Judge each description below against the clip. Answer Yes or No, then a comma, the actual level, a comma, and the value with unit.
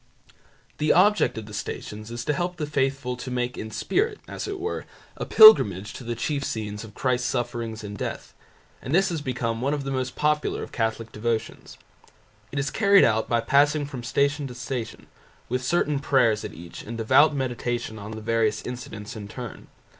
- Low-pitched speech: Yes, low, 125 Hz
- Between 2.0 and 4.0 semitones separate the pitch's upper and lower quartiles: No, average, 4.4 semitones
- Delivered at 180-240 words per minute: Yes, average, 190 wpm